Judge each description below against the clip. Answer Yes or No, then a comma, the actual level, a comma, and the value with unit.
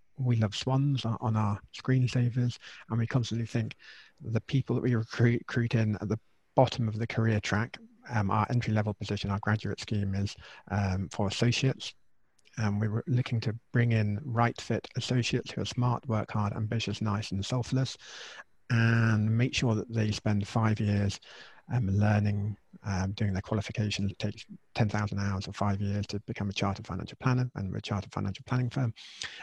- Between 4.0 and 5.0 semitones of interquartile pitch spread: No, average, 2.8 semitones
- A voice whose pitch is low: Yes, low, 110 Hz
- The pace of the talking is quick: No, average, 175 wpm